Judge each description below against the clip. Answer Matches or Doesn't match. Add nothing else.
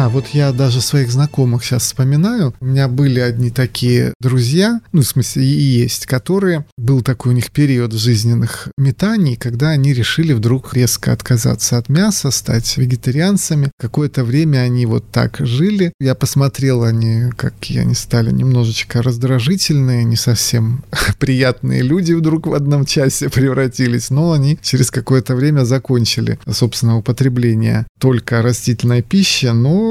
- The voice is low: Matches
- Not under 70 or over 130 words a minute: Doesn't match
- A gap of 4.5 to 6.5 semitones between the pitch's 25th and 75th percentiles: Doesn't match